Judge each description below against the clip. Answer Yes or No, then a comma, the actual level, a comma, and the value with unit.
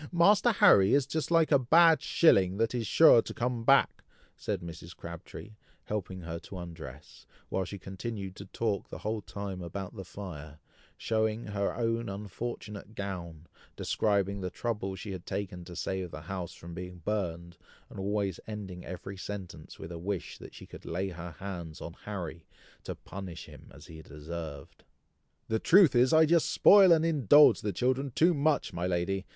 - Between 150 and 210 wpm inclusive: Yes, average, 175 wpm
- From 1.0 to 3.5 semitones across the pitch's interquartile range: No, average, 4.8 semitones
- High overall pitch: No, low, 100 Hz